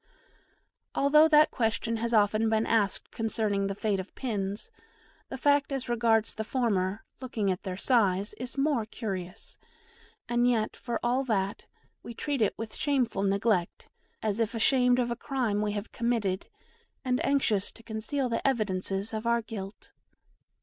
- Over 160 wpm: No, average, 155 wpm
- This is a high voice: Yes, high, 225 Hz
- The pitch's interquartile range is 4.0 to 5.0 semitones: No, average, 3.4 semitones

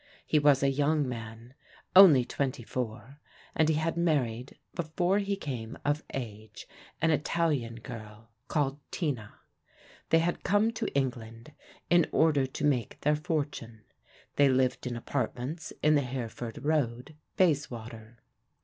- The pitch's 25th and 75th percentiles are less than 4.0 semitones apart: No, average, 4.7 semitones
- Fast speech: No, slow, 135 wpm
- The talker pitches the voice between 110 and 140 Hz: Yes, low, 135 Hz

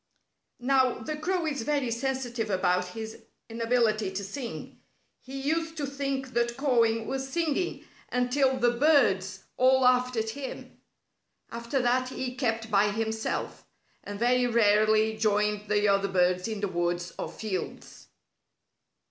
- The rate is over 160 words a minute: No, average, 140 wpm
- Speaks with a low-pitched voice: No, high, 235 Hz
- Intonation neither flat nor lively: Yes, average, 4.0 semitones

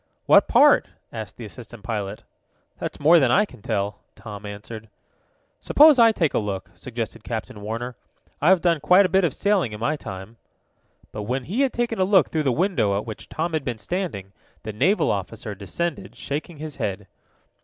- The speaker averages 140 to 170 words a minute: No, average, 185 wpm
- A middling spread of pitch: No, wide, 8.5 semitones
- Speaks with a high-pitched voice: No, low, 120 Hz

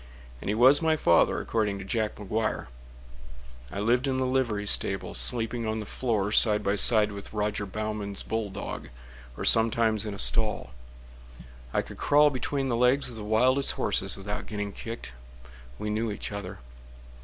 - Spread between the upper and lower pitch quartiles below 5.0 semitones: Yes, average, 2.7 semitones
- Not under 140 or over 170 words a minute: Yes, average, 165 wpm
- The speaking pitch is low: Yes, low, 110 Hz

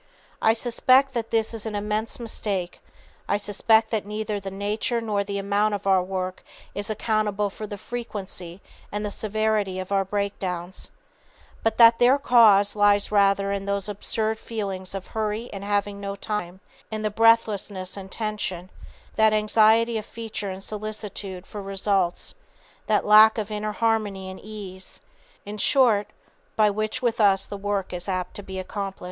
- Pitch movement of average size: No, narrow, 1.8 semitones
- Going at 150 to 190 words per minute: Yes, average, 165 wpm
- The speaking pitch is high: Yes, high, 205 Hz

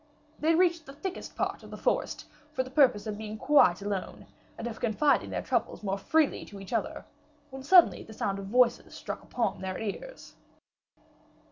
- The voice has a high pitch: Yes, high, 235 Hz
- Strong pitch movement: Yes, wide, 6.5 semitones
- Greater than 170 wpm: Yes, average, 180 wpm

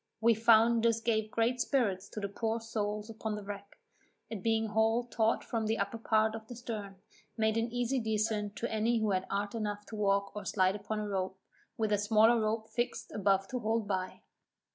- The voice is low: No, high, 220 Hz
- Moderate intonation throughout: No, narrow, 1.8 semitones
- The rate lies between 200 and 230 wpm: Yes, fast, 205 wpm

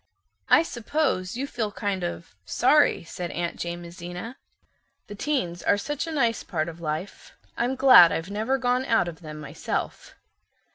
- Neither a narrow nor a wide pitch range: No, wide, 6.8 semitones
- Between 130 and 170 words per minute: Yes, average, 155 wpm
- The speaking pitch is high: Yes, high, 200 Hz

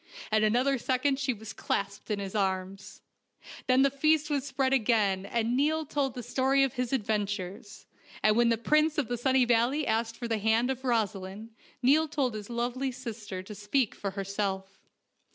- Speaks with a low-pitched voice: No, high, 235 Hz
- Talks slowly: No, average, 180 wpm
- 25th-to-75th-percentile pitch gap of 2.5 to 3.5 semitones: No, average, 4.4 semitones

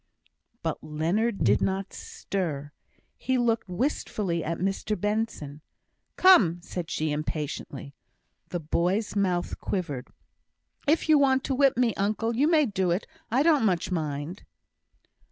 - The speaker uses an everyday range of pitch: No, wide, 6.0 semitones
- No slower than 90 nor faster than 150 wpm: Yes, slow, 135 wpm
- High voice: Yes, high, 195 Hz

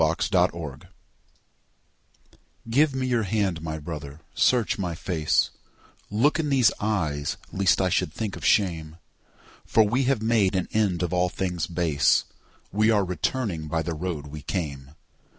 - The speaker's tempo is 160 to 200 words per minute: No, average, 145 wpm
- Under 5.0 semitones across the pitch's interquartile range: No, average, 5.3 semitones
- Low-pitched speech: Yes, very low, 90 Hz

